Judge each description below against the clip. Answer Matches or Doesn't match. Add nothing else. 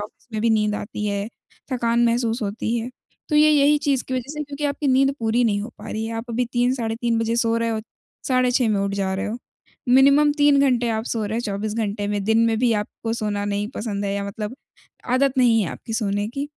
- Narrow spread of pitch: Doesn't match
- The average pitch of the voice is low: Doesn't match